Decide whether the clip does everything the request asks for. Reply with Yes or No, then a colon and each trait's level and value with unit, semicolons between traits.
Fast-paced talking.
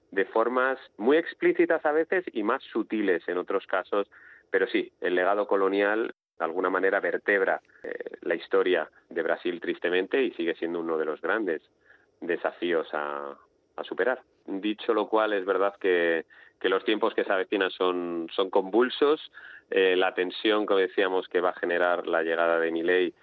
No: average, 170 wpm